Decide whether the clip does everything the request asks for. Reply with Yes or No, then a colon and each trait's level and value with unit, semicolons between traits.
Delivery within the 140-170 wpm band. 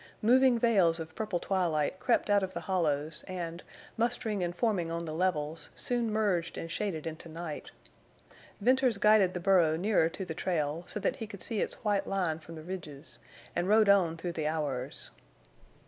No: average, 180 wpm